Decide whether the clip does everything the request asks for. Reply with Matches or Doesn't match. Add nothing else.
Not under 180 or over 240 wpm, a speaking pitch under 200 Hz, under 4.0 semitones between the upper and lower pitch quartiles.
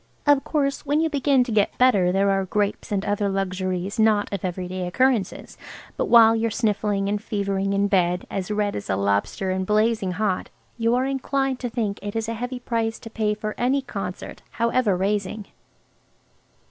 Doesn't match